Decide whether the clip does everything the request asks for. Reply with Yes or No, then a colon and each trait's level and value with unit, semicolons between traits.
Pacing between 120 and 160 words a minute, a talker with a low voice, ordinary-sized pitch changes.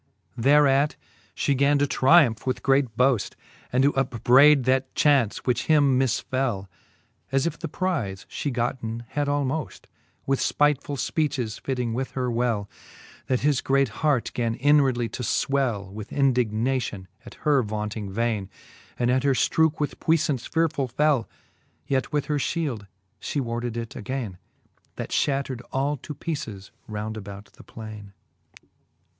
Yes: average, 150 wpm; low, 130 Hz; average, 3.8 semitones